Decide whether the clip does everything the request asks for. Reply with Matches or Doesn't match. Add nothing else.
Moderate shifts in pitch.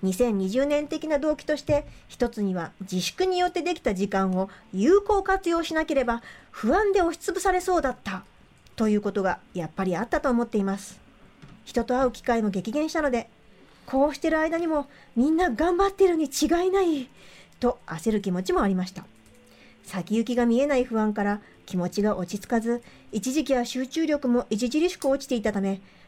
Doesn't match